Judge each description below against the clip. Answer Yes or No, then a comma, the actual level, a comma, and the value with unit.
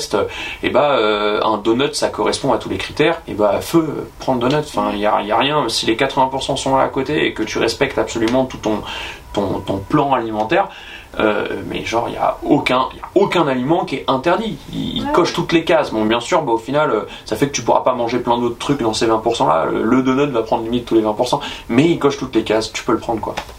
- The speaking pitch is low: Yes, low, 120 Hz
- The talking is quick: Yes, fast, 245 wpm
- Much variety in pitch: No, average, 3.6 semitones